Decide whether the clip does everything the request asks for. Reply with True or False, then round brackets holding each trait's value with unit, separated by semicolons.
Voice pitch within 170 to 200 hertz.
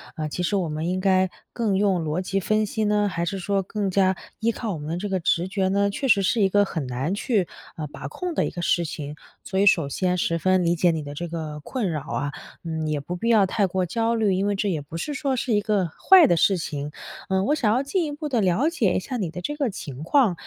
True (190 Hz)